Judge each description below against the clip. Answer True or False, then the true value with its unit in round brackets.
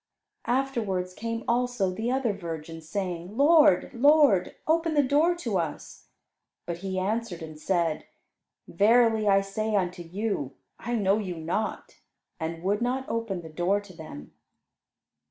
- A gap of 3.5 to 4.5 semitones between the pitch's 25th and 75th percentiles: False (5.3 semitones)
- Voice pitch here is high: True (200 Hz)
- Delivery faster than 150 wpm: False (140 wpm)